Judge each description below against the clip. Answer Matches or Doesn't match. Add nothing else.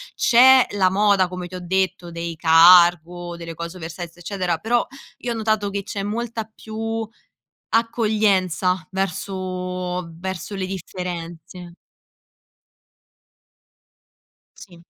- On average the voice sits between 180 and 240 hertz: Matches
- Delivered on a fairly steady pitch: Doesn't match